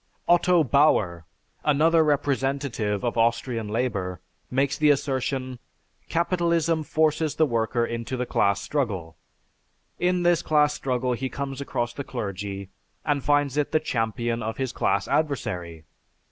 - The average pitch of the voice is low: Yes, low, 130 Hz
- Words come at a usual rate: No, slow, 130 wpm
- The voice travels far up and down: No, average, 4.8 semitones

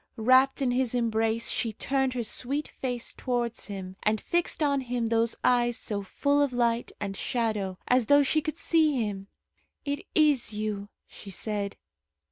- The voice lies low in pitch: No, high, 240 Hz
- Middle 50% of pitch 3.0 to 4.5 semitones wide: Yes, average, 4.0 semitones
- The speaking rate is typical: Yes, average, 165 wpm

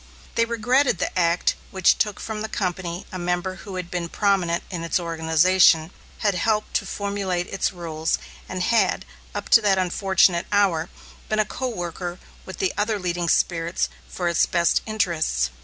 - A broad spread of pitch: No, average, 3.0 semitones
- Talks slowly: No, average, 170 wpm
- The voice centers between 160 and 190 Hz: Yes, medium, 185 Hz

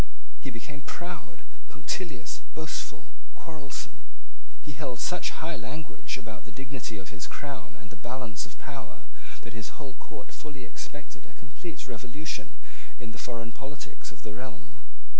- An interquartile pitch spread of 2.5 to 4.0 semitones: No, average, 4.8 semitones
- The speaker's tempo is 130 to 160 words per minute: Yes, average, 150 wpm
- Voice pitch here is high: No, low, 125 Hz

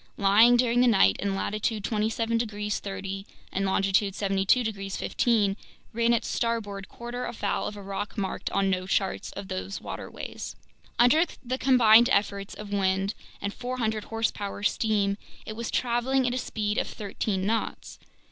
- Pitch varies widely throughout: No, average, 2.9 semitones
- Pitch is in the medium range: No, high, 210 Hz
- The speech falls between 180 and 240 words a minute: No, average, 155 wpm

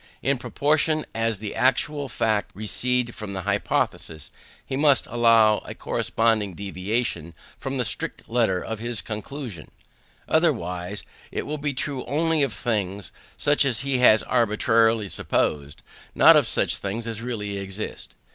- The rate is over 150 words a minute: No, average, 145 wpm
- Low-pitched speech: Yes, low, 115 Hz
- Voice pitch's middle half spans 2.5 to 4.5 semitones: Yes, average, 4.2 semitones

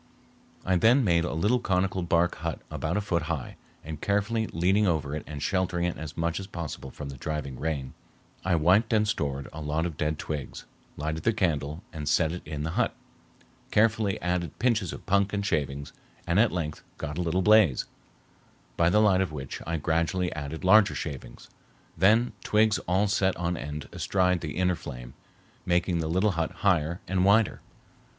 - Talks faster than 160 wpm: Yes, average, 185 wpm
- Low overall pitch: Yes, very low, 85 Hz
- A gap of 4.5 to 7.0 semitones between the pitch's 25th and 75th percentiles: No, average, 4.0 semitones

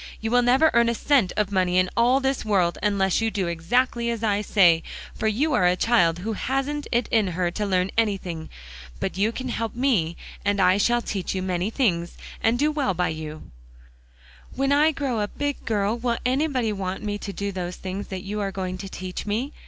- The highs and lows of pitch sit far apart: No, average, 4.6 semitones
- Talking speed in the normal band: No, fast, 215 wpm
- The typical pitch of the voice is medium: No, high, 210 Hz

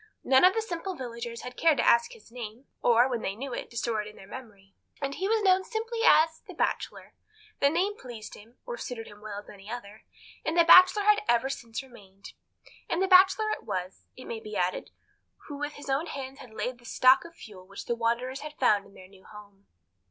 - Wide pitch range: Yes, wide, 7.5 semitones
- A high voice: Yes, very high, 250 Hz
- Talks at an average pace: No, fast, 240 wpm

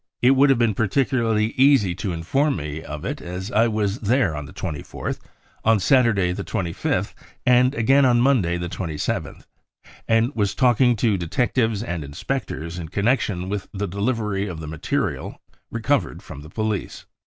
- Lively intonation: Yes, wide, 5.8 semitones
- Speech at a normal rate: Yes, average, 165 wpm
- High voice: No, low, 105 Hz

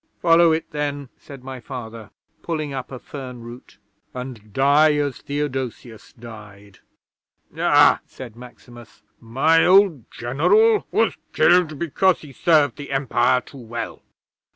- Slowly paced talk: Yes, slow, 130 wpm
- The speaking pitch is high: No, low, 135 Hz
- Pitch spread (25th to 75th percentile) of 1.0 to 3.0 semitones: No, average, 4.2 semitones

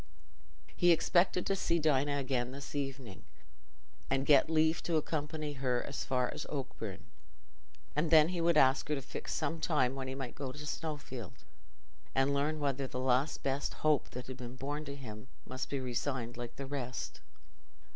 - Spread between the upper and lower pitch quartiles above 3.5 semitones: No, average, 2.8 semitones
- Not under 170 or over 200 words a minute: Yes, average, 175 wpm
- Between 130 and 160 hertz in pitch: Yes, medium, 140 Hz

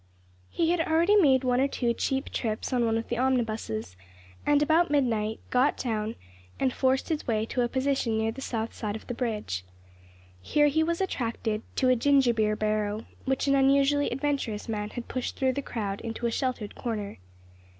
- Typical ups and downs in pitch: Yes, average, 3.9 semitones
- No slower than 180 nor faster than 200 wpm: Yes, average, 190 wpm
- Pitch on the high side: Yes, high, 245 Hz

